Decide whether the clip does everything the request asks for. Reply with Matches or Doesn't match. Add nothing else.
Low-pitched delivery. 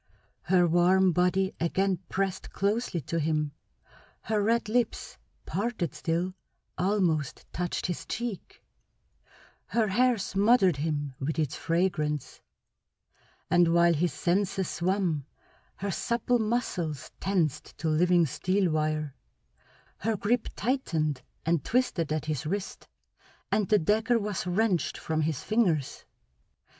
Doesn't match